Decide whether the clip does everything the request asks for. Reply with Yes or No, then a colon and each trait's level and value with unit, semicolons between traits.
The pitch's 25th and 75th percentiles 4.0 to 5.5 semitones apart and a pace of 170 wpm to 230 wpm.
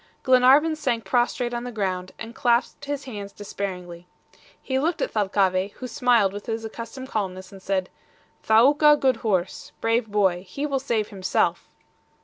No: average, 4.7 semitones; average, 155 wpm